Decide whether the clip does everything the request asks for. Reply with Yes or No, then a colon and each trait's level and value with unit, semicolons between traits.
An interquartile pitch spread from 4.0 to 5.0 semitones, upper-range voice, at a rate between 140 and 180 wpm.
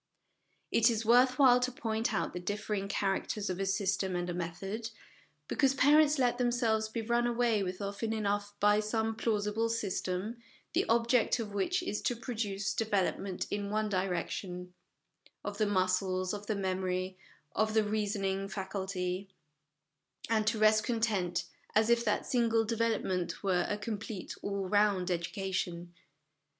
No: average, 3.0 semitones; high, 205 Hz; average, 155 wpm